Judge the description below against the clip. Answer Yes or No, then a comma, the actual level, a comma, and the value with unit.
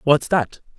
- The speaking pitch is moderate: Yes, medium, 145 Hz